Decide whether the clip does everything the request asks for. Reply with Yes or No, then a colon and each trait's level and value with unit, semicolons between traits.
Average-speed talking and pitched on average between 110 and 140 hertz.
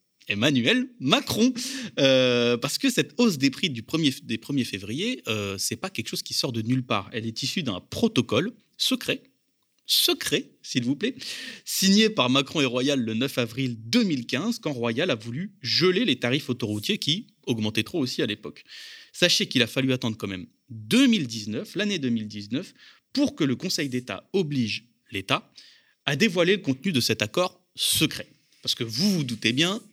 Yes: average, 180 wpm; low, 135 Hz